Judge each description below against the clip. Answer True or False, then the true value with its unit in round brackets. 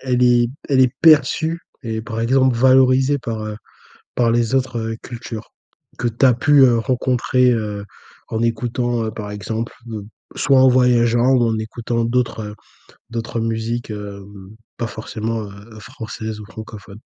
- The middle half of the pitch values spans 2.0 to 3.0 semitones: True (2.4 semitones)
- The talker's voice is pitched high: False (115 Hz)